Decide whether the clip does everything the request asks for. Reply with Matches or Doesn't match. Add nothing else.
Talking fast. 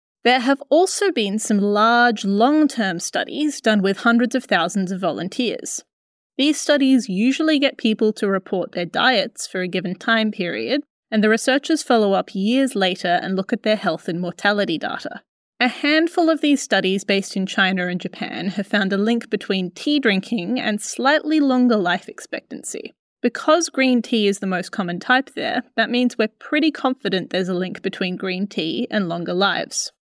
Doesn't match